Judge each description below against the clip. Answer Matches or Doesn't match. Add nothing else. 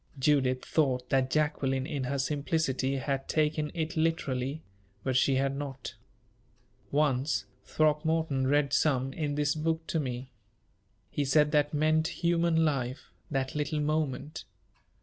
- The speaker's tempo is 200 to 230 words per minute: Doesn't match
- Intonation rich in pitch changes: Doesn't match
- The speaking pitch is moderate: Matches